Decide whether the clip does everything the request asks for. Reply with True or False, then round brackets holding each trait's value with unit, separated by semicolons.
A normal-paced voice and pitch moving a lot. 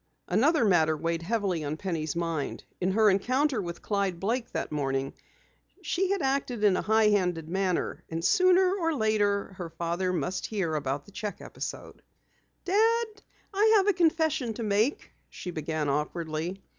True (160 wpm; 7.4 semitones)